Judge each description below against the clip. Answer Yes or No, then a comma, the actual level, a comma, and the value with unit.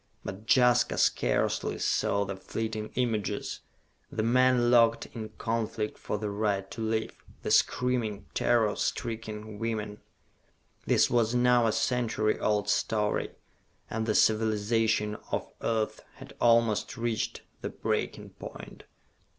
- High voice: No, low, 110 Hz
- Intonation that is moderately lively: No, narrow, 1.7 semitones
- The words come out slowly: Yes, slow, 125 wpm